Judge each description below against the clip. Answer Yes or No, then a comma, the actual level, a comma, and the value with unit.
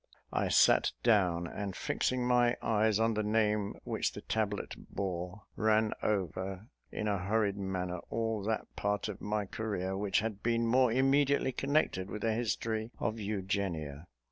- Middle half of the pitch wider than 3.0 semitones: No, narrow, 2.6 semitones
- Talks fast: No, average, 155 wpm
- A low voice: Yes, low, 105 Hz